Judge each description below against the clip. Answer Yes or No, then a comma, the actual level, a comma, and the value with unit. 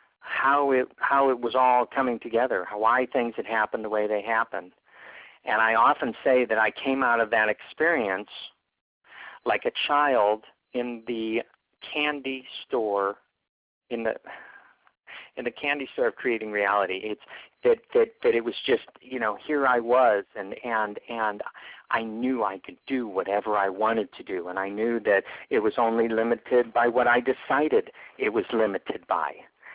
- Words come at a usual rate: Yes, average, 175 wpm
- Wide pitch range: No, average, 3.7 semitones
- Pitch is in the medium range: No, low, 120 Hz